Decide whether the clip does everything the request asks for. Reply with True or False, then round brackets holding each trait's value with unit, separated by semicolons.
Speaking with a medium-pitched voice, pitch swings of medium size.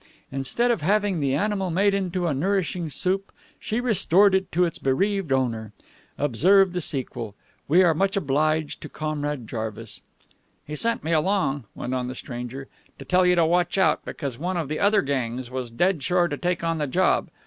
False (165 Hz; 5.8 semitones)